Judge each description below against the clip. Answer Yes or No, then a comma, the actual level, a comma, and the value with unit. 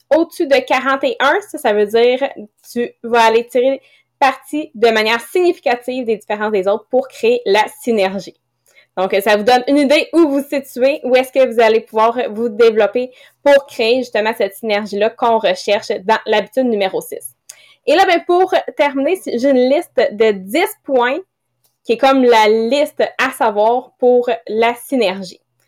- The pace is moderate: Yes, average, 175 wpm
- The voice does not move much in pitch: No, average, 4.1 semitones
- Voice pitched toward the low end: No, high, 245 Hz